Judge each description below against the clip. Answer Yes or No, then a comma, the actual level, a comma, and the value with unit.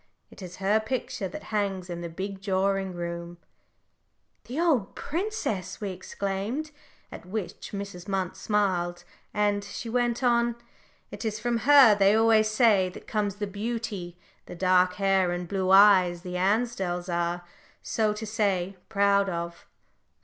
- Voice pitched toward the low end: No, high, 200 Hz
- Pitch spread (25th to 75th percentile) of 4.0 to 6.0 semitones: No, average, 3.1 semitones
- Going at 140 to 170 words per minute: Yes, average, 150 wpm